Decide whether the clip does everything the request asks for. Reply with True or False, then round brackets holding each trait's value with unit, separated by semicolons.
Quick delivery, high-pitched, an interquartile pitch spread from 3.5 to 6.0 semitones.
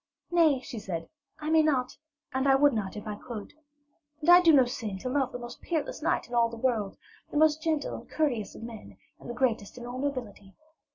True (225 wpm; 255 Hz; 4.8 semitones)